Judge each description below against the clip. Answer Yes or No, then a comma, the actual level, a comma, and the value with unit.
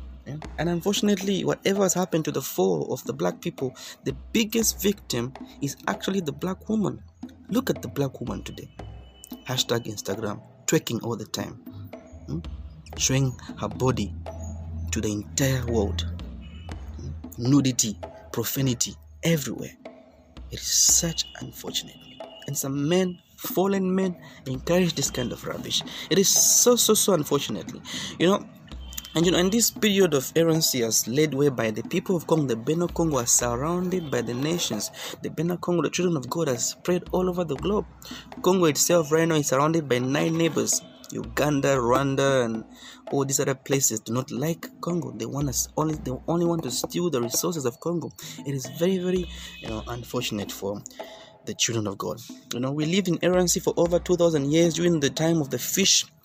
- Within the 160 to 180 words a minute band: Yes, average, 175 wpm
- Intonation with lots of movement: Yes, wide, 6.5 semitones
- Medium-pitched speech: Yes, medium, 145 Hz